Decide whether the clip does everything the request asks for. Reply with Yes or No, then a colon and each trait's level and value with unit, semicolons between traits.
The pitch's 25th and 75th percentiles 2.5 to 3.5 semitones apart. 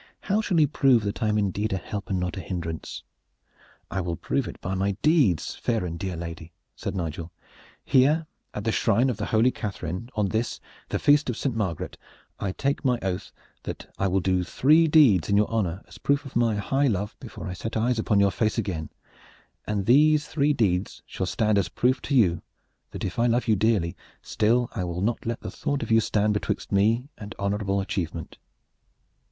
No: average, 4.6 semitones